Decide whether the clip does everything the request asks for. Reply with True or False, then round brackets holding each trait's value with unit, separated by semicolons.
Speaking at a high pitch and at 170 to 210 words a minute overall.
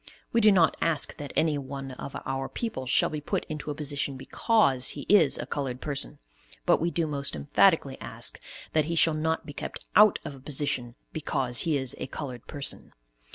False (145 Hz; 195 wpm)